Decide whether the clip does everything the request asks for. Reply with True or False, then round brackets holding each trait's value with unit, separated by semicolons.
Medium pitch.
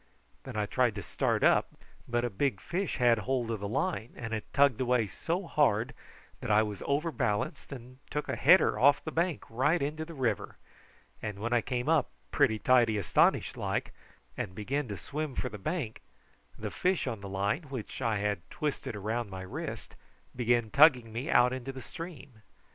False (125 Hz)